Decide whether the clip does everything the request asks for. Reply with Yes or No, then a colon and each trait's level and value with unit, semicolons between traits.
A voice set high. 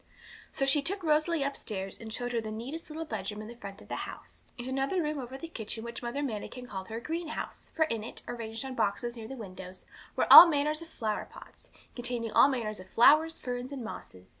Yes: high, 245 Hz